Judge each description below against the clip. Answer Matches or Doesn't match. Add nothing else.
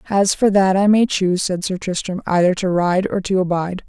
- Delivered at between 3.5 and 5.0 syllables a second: Doesn't match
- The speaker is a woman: Matches